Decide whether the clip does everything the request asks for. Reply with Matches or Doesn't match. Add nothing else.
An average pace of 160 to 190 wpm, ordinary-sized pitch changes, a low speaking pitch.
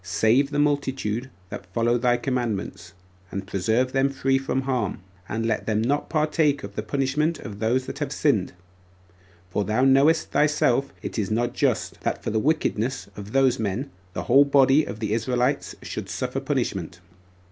Matches